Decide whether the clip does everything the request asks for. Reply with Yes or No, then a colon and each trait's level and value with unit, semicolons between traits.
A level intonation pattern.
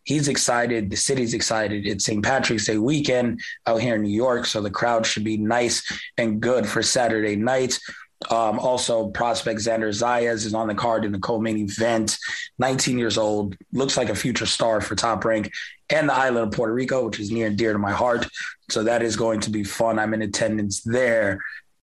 Yes: narrow, 1.9 semitones